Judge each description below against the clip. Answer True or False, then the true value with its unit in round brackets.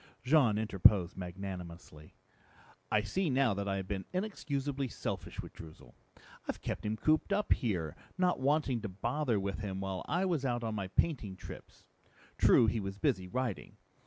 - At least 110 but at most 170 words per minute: True (165 wpm)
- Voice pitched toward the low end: True (105 Hz)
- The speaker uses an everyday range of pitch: False (6.3 semitones)